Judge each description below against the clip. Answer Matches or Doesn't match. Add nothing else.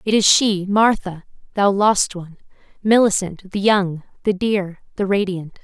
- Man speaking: Doesn't match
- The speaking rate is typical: Matches